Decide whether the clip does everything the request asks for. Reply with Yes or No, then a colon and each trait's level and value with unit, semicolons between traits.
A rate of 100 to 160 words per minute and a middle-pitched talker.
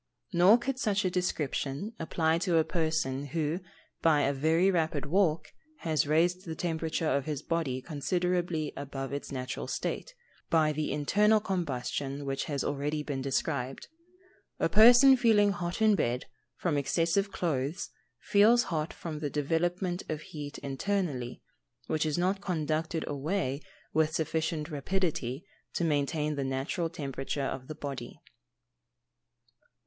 Yes: average, 140 wpm; medium, 160 Hz